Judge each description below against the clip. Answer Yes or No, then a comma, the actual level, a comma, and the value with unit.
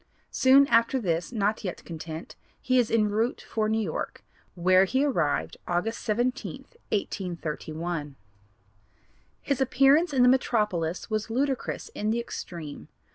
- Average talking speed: No, slow, 130 wpm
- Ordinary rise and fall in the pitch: No, wide, 6.3 semitones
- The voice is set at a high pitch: Yes, high, 215 Hz